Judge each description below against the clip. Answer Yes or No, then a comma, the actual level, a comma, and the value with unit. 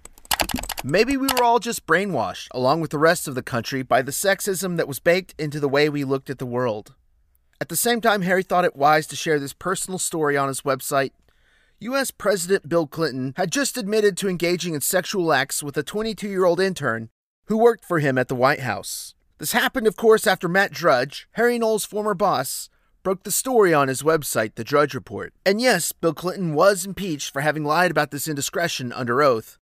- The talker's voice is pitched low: No, medium, 165 Hz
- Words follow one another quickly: Yes, fast, 210 wpm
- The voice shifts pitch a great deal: Yes, wide, 5.9 semitones